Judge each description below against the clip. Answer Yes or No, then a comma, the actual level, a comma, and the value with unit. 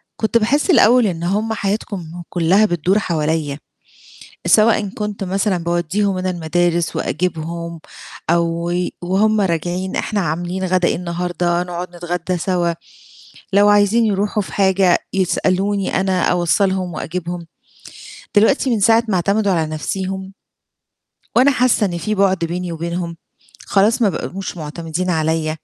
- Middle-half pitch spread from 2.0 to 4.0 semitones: Yes, average, 3.0 semitones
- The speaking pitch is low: No, medium, 185 Hz